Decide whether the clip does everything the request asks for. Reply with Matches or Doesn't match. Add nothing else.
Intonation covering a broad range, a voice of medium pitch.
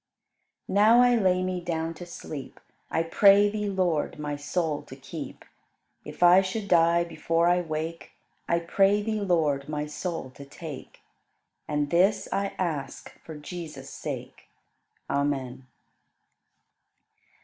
Doesn't match